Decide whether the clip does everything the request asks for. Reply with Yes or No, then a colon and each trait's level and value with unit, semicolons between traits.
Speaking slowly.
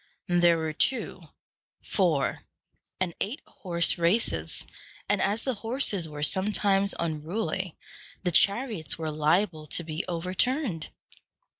Yes: slow, 115 wpm